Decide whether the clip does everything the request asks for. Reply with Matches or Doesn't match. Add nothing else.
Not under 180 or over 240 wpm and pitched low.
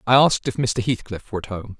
Doesn't match